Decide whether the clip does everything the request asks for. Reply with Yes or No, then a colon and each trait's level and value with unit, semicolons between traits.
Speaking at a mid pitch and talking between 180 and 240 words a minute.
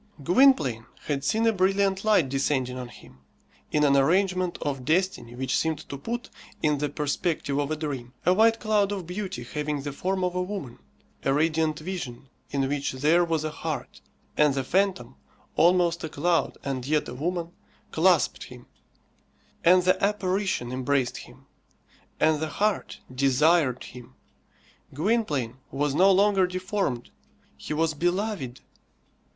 No: medium, 155 Hz; average, 150 wpm